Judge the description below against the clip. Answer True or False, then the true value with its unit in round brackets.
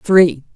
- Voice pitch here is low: False (170 Hz)